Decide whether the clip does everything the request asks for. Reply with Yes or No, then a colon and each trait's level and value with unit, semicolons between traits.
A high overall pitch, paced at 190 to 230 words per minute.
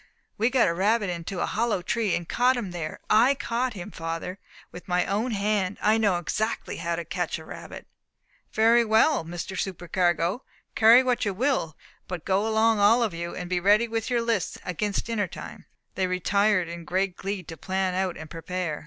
Yes: high, 195 Hz; average, 195 wpm